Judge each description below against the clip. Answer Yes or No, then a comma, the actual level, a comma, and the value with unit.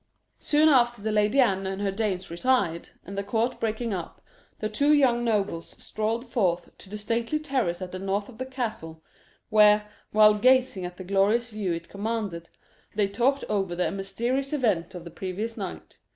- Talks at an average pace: Yes, average, 180 wpm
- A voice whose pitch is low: No, high, 210 Hz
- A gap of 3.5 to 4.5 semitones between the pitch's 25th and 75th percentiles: Yes, average, 3.9 semitones